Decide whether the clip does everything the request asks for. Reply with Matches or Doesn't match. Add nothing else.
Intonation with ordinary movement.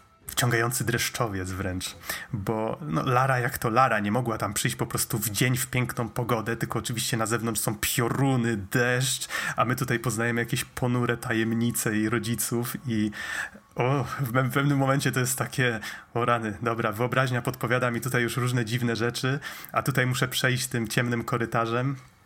Doesn't match